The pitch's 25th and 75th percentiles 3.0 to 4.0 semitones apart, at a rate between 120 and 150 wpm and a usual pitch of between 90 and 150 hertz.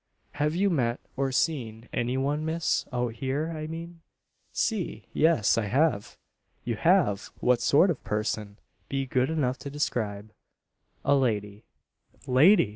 No: wide, 5.6 semitones; average, 145 wpm; low, 135 Hz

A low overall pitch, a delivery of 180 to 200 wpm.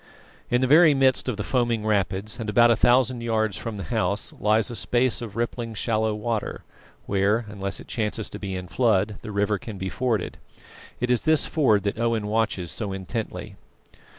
Yes: low, 110 Hz; average, 190 wpm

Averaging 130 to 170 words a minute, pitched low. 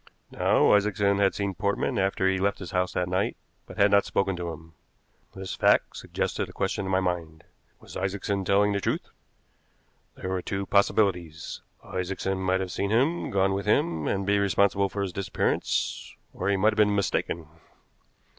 No: average, 185 wpm; very low, 95 Hz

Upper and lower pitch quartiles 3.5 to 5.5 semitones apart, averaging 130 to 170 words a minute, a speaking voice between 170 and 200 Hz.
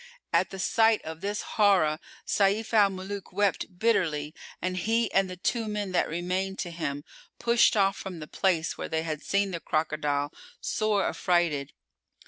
Yes: average, 4.0 semitones; average, 165 wpm; medium, 185 Hz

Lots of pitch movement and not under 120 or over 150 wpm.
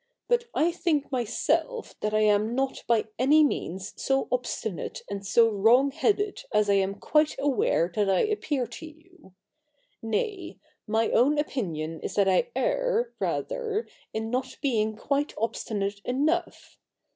Yes: wide, 7.0 semitones; average, 145 wpm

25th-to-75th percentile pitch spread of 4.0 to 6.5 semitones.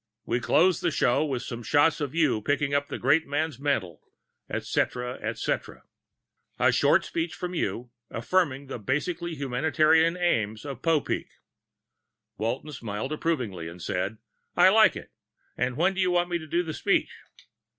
Yes: average, 5.1 semitones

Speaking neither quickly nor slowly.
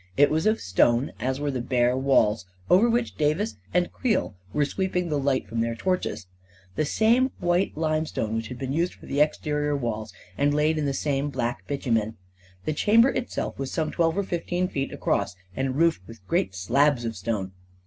Yes: average, 195 wpm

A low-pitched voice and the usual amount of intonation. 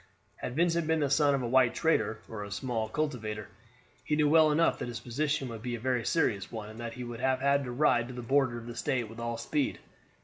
Yes: low, 125 Hz; average, 3.9 semitones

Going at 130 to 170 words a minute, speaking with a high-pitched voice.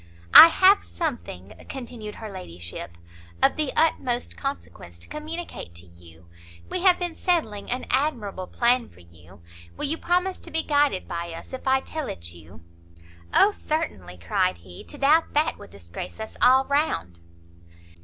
Yes: average, 160 wpm; high, 240 Hz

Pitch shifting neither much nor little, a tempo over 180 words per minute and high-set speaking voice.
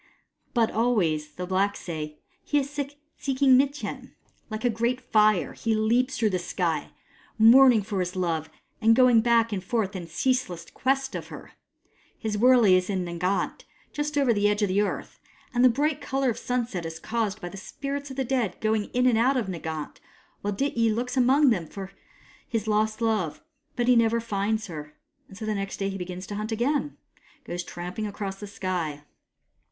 Yes: average, 5.0 semitones; average, 190 wpm; high, 215 Hz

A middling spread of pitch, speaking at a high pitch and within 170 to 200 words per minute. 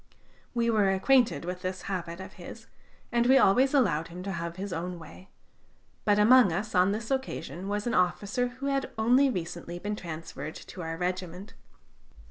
Yes: average, 5.0 semitones; high, 195 Hz; average, 175 wpm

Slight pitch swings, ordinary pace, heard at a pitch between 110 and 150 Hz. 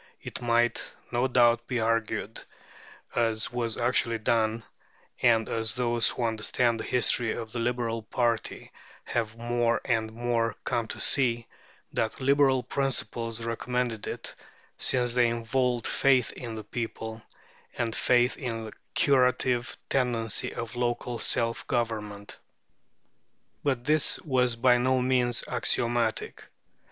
No: narrow, 1.5 semitones; slow, 125 wpm; low, 120 Hz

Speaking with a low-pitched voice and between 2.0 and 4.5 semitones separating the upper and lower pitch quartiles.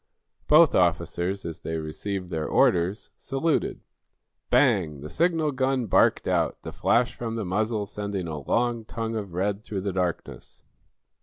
No: low, 100 Hz; average, 5.2 semitones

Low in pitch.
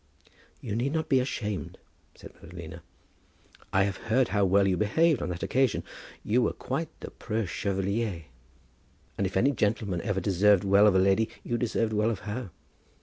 Yes: low, 105 Hz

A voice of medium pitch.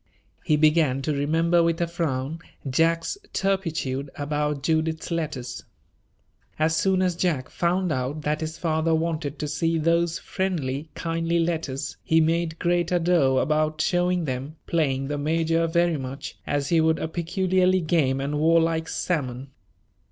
Yes: medium, 160 Hz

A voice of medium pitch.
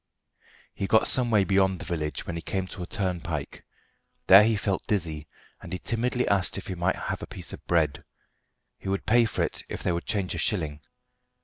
No: very low, 95 Hz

